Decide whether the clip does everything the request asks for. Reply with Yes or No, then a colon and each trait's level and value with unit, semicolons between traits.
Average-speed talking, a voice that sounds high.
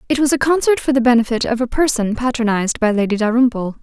No: fast, 220 wpm; high, 240 Hz